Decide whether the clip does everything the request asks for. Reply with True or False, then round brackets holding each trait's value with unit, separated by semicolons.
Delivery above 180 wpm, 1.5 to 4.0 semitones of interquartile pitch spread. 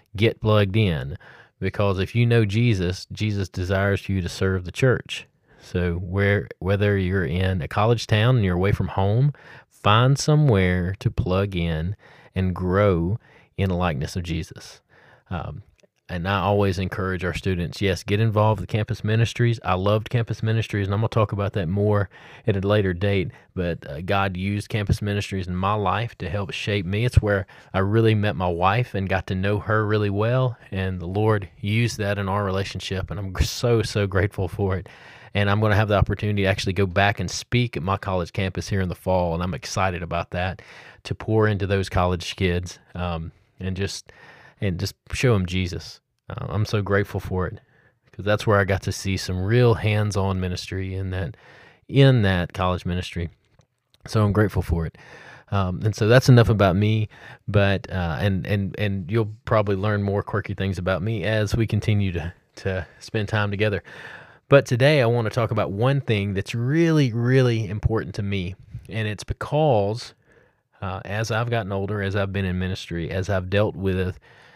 True (190 wpm; 2.8 semitones)